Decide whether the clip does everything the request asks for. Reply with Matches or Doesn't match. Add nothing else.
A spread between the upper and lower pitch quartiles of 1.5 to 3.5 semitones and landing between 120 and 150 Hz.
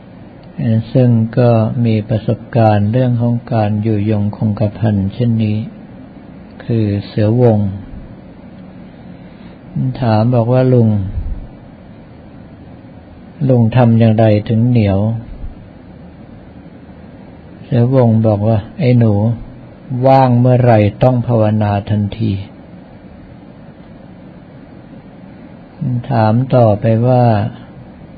Doesn't match